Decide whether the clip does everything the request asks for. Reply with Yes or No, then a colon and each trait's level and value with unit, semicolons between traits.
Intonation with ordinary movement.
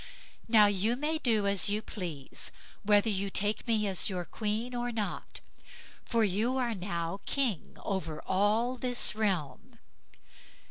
Yes: average, 3.3 semitones